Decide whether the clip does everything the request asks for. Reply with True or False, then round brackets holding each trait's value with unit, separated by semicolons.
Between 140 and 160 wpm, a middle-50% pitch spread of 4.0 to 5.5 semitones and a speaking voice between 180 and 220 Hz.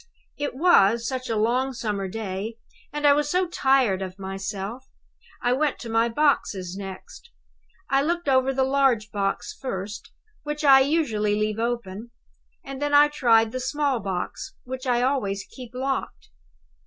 False (155 wpm; 4.7 semitones; 245 Hz)